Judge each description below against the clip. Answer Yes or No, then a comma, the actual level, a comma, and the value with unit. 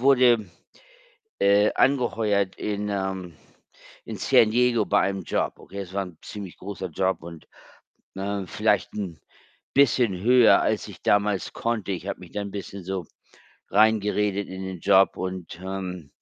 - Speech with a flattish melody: Yes, narrow, 2.2 semitones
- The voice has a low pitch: Yes, low, 100 Hz